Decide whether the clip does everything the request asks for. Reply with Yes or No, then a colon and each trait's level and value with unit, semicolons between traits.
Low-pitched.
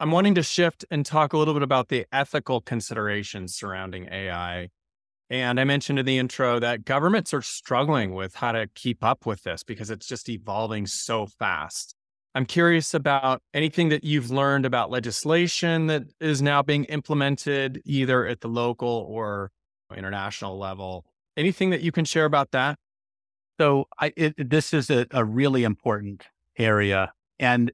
Yes: low, 130 Hz